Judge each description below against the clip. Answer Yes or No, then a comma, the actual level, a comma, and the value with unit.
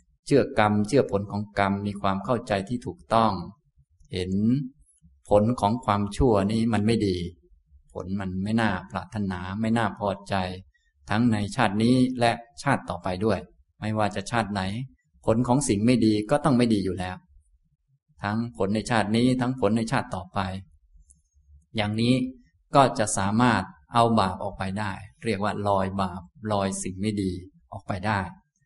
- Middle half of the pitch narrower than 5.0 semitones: Yes, average, 3.6 semitones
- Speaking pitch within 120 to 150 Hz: No, low, 100 Hz